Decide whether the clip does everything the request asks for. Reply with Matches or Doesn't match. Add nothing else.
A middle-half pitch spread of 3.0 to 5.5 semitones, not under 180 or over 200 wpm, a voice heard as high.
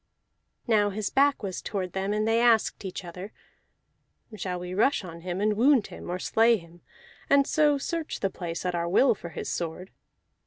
Matches